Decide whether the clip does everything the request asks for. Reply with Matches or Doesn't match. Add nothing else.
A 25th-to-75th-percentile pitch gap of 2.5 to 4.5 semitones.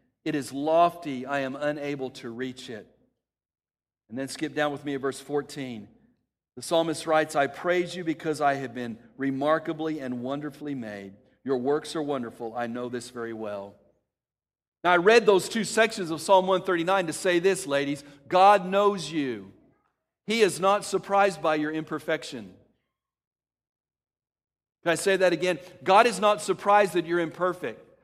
Doesn't match